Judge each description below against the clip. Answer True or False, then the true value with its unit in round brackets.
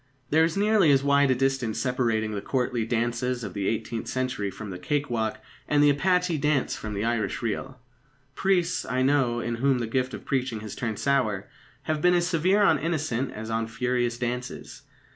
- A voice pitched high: False (125 Hz)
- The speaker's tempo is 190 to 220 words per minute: True (195 wpm)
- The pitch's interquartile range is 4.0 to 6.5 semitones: True (4.3 semitones)